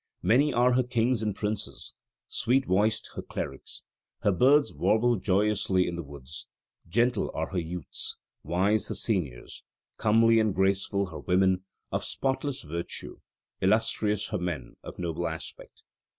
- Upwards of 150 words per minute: No, average, 140 wpm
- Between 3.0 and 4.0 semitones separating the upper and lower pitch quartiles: No, average, 4.4 semitones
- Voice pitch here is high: No, low, 100 Hz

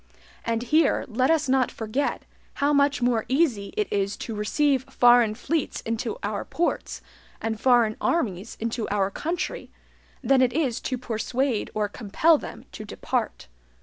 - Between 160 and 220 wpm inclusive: No, average, 150 wpm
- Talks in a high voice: Yes, high, 245 Hz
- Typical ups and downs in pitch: Yes, average, 4.5 semitones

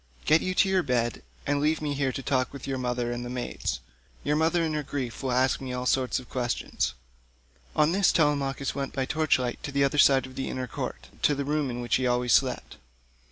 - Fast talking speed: Yes, fast, 235 wpm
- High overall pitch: No, low, 135 Hz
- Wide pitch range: No, average, 2.8 semitones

